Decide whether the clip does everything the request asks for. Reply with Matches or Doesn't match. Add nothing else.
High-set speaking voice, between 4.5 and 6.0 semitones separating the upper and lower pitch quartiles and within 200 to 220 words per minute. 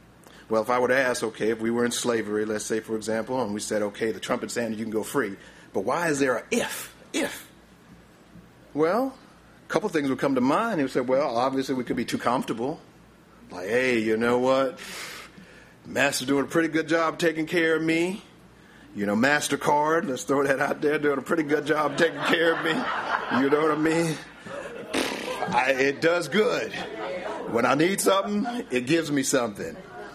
Doesn't match